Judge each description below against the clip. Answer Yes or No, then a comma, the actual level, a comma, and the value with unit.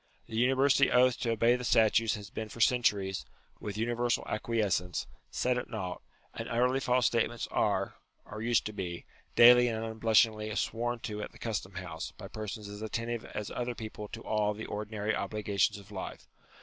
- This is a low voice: Yes, low, 110 Hz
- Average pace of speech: Yes, average, 180 wpm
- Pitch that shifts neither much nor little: No, narrow, 2.3 semitones